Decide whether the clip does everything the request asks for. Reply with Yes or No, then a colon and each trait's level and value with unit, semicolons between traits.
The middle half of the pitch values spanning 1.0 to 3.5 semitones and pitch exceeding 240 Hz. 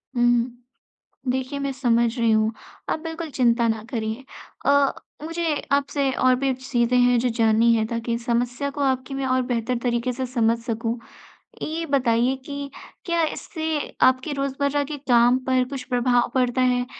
Yes: average, 2.8 semitones; very high, 250 Hz